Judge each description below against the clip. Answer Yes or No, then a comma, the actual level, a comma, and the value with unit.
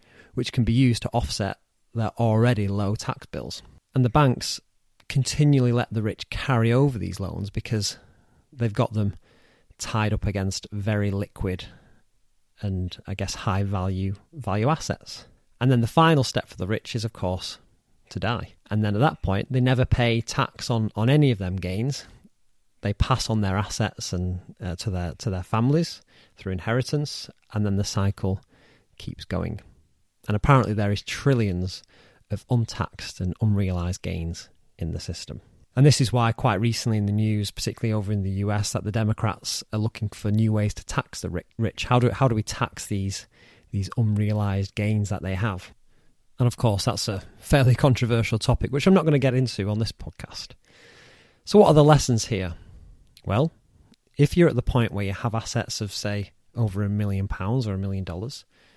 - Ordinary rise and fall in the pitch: Yes, average, 3.7 semitones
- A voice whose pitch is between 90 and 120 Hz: Yes, low, 110 Hz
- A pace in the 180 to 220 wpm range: Yes, average, 185 wpm